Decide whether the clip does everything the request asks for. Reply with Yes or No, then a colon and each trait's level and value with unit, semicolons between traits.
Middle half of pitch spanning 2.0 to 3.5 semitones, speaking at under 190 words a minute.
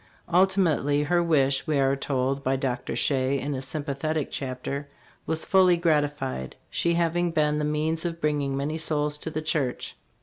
Yes: average, 2.8 semitones; average, 170 wpm